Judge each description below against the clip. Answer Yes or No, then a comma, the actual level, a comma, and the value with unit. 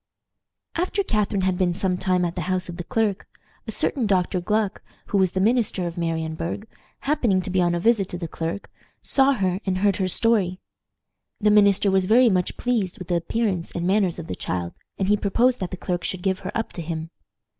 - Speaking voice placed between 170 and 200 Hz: Yes, high, 190 Hz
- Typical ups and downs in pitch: Yes, average, 3.2 semitones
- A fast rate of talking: Yes, fast, 215 wpm